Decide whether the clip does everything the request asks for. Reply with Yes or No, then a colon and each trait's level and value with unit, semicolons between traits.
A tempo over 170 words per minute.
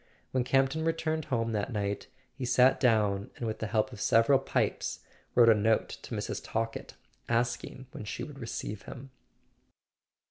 No: average, 165 wpm